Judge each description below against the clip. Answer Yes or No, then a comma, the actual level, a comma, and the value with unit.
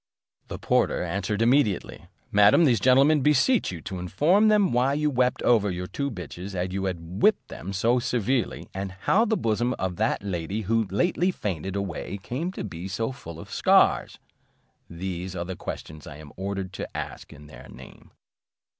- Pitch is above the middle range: No, low, 100 Hz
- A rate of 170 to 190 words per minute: Yes, average, 180 wpm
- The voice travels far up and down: Yes, wide, 5.8 semitones